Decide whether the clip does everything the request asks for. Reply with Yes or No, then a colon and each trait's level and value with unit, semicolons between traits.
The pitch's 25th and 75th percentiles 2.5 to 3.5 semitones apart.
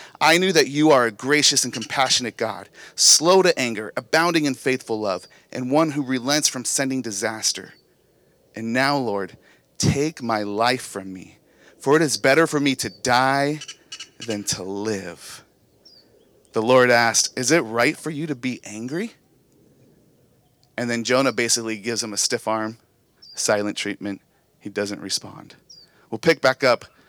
No: average, 4.6 semitones